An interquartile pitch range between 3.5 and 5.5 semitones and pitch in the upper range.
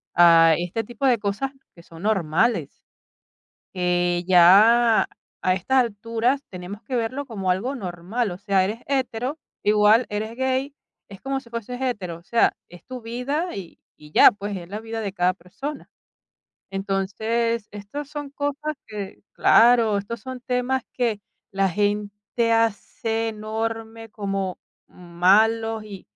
Yes: average, 3.8 semitones; high, 220 Hz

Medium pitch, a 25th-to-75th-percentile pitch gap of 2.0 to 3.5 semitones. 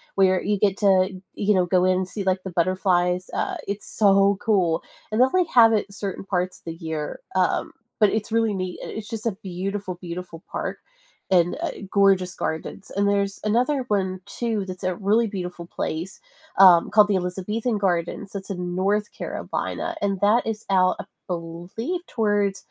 No: high, 195 Hz; narrow, 2.5 semitones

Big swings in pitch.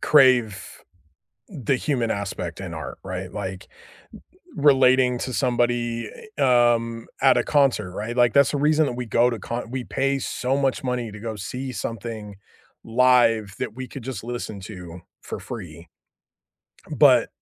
No: average, 3.2 semitones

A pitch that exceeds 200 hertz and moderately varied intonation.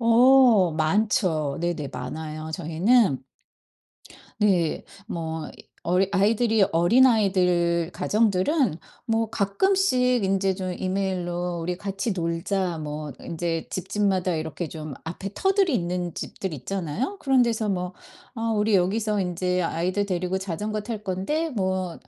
No: high, 190 Hz; average, 4.1 semitones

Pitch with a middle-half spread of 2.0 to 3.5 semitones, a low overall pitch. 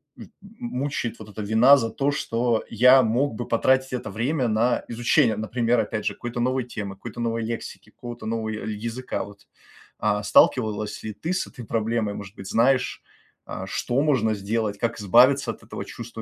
Yes: average, 2.7 semitones; low, 115 Hz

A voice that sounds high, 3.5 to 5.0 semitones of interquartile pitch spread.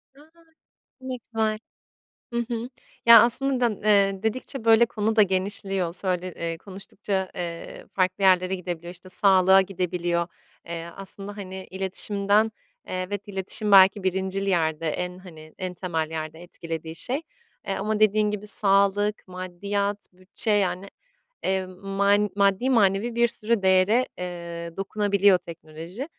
No: high, 195 Hz; narrow, 2.5 semitones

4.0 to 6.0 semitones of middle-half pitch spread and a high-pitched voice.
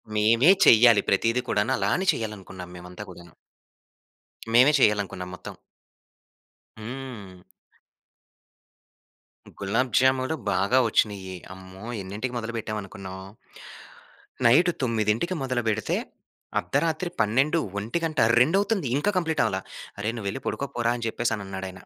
No: average, 5.0 semitones; low, 115 Hz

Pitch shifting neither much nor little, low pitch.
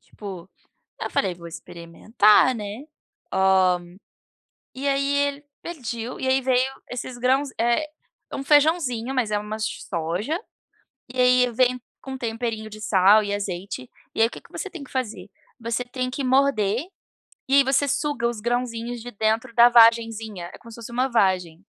No: average, 3.7 semitones; high, 235 Hz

